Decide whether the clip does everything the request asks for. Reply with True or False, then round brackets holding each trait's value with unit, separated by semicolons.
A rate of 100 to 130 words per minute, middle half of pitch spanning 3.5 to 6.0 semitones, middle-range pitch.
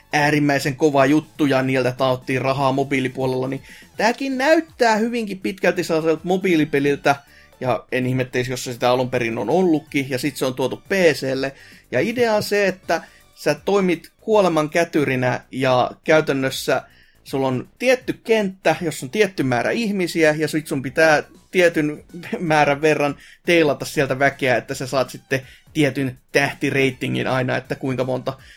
False (150 wpm; 4.3 semitones; 145 Hz)